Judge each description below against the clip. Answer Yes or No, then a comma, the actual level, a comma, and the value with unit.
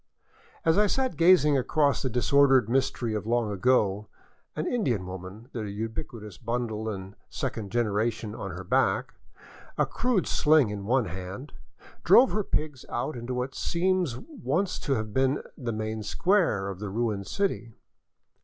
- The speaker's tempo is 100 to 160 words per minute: Yes, average, 155 wpm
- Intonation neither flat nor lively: No, wide, 6.0 semitones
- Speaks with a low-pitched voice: Yes, low, 120 Hz